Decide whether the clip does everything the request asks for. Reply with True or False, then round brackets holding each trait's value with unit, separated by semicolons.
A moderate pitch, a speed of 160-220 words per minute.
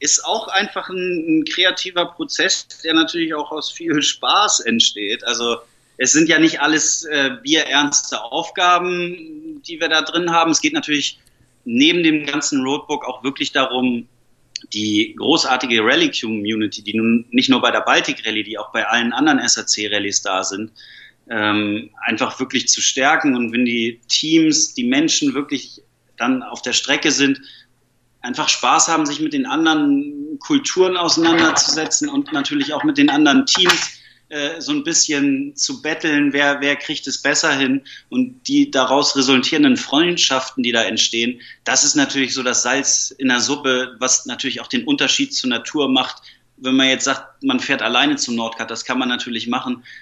True (155 Hz; 170 wpm)